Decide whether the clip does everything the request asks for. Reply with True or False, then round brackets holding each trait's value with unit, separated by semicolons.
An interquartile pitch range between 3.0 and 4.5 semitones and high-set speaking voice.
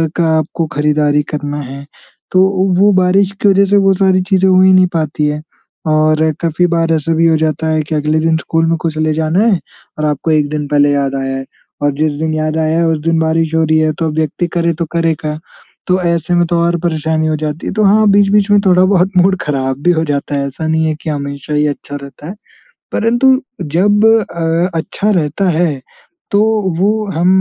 False (3.4 semitones; 160 Hz)